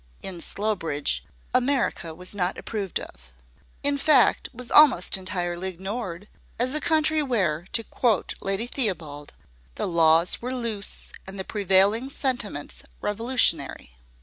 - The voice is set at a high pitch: Yes, high, 200 Hz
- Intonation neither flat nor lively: No, wide, 6.0 semitones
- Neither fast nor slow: No, slow, 125 wpm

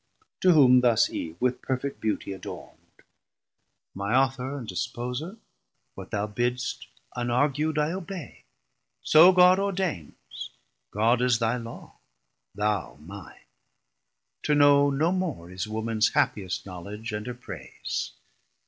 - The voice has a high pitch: No, low, 125 Hz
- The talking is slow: Yes, slow, 120 wpm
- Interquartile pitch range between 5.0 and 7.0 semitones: Yes, wide, 5.6 semitones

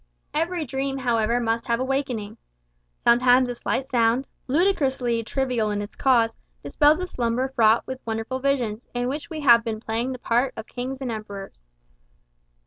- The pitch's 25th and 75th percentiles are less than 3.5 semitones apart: Yes, average, 2.8 semitones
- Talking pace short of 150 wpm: No, average, 165 wpm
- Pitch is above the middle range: Yes, high, 245 Hz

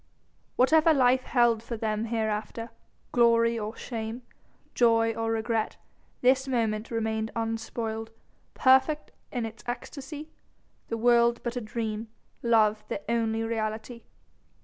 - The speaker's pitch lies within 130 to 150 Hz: No, high, 230 Hz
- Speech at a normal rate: No, slow, 120 wpm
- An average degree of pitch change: No, narrow, 1.6 semitones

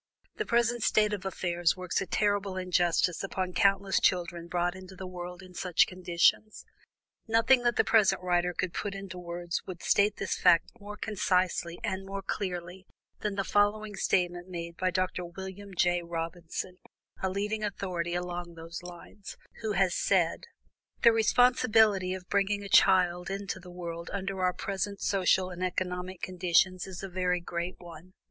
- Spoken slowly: No, average, 160 wpm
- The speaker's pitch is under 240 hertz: Yes, medium, 185 Hz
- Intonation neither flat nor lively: No, narrow, 2.0 semitones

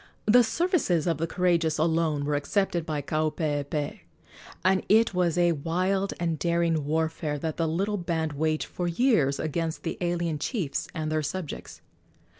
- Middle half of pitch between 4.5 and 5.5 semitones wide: No, narrow, 2.6 semitones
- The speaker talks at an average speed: Yes, average, 155 wpm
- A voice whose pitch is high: No, medium, 165 Hz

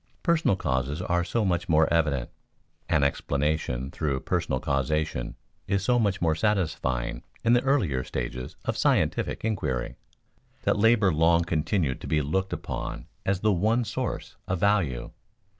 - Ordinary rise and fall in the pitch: No, wide, 6.4 semitones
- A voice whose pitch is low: Yes, very low, 85 Hz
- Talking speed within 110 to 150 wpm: Yes, average, 145 wpm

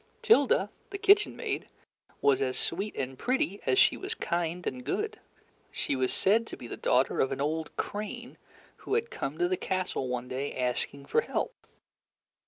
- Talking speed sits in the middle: Yes, average, 180 wpm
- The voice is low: No, medium, 175 Hz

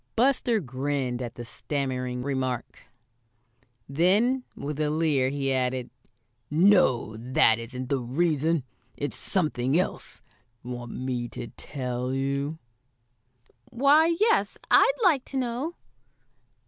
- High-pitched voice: No, medium, 140 Hz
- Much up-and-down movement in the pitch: Yes, wide, 6.2 semitones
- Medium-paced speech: No, slow, 110 wpm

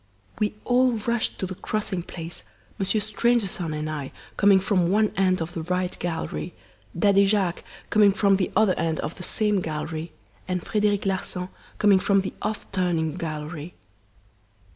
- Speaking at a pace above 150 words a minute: Yes, average, 160 wpm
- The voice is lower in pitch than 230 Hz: Yes, high, 190 Hz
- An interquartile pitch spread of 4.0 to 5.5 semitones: No, average, 3.6 semitones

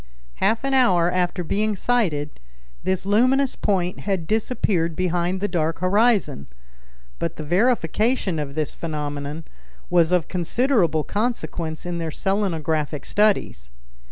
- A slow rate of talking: Yes, slow, 125 wpm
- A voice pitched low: No, medium, 180 Hz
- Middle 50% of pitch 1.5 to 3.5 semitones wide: No, average, 4.8 semitones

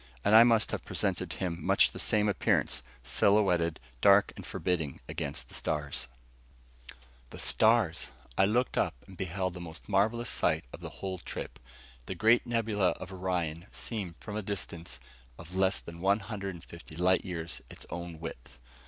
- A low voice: Yes, very low, 95 Hz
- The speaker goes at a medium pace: Yes, average, 170 wpm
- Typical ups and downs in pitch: Yes, average, 3.6 semitones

